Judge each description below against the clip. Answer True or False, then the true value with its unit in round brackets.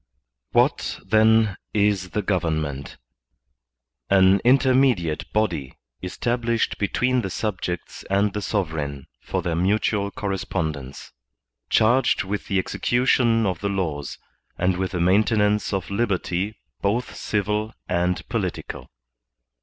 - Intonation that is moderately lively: True (3.5 semitones)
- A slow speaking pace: True (115 wpm)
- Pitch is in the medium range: False (100 Hz)